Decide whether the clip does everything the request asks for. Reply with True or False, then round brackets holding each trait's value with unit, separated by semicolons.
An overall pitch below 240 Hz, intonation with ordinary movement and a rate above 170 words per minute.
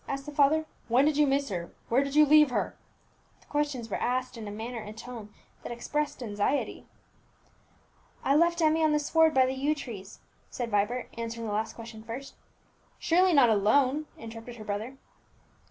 False (255 Hz; 4.7 semitones; 185 wpm)